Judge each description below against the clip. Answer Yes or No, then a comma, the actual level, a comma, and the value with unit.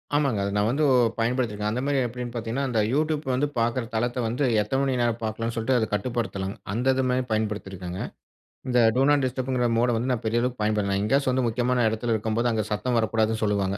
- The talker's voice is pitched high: No, low, 120 Hz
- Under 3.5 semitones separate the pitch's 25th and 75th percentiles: Yes, average, 2.7 semitones